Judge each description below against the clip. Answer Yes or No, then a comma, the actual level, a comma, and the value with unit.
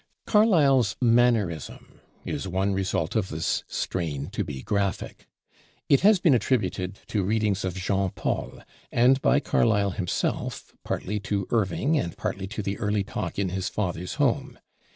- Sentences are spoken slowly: No, average, 150 wpm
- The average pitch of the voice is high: No, low, 100 Hz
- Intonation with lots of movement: No, average, 4.0 semitones